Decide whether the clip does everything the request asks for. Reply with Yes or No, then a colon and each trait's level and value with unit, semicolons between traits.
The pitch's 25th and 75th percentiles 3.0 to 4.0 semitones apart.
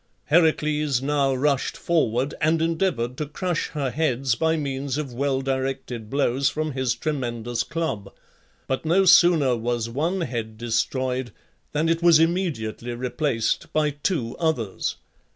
No: average, 4.6 semitones